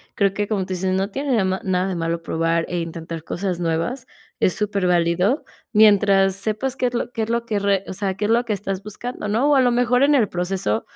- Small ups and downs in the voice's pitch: No, average, 4.2 semitones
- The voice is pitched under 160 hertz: No, high, 195 Hz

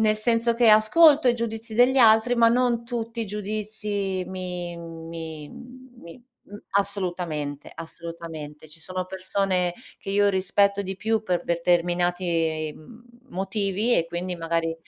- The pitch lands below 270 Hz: Yes, high, 190 Hz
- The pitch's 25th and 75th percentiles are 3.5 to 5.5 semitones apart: Yes, average, 4.5 semitones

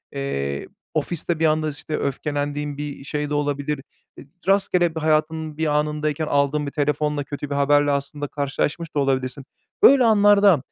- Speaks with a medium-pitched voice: Yes, medium, 150 Hz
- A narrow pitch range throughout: Yes, narrow, 1.8 semitones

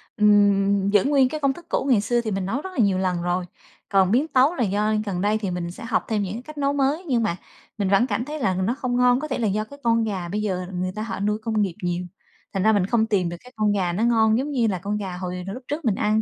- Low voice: No, high, 215 Hz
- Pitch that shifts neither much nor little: Yes, average, 4.2 semitones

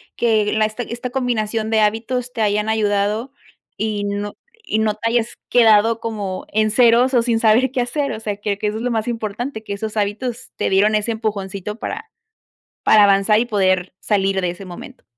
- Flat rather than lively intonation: Yes, narrow, 2.3 semitones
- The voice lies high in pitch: Yes, high, 215 Hz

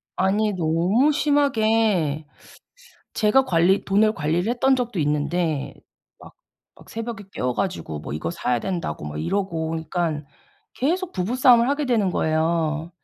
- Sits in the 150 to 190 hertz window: Yes, medium, 185 Hz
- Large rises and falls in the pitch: Yes, wide, 6.3 semitones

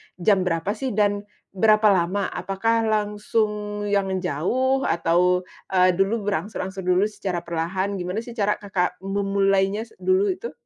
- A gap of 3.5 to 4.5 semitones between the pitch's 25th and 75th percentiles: No, narrow, 2.6 semitones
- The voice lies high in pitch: Yes, high, 200 Hz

